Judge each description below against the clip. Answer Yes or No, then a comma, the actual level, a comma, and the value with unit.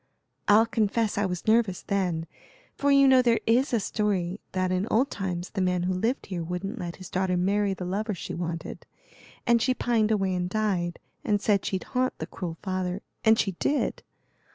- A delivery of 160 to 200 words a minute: Yes, average, 195 wpm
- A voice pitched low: No, high, 195 Hz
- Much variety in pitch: No, average, 3.6 semitones